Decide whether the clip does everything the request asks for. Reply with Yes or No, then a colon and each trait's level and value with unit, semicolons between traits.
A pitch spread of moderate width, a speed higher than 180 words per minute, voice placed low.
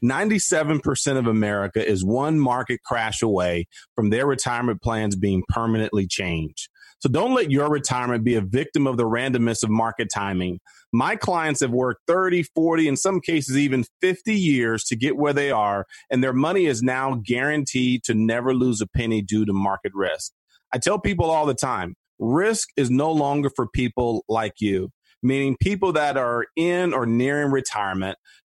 No: average, 4.5 semitones; average, 175 wpm; low, 125 Hz